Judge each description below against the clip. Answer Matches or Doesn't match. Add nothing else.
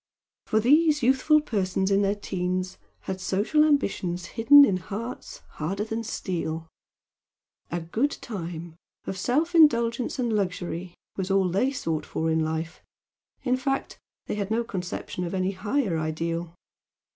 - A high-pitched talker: Matches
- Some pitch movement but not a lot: Doesn't match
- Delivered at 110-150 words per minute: Matches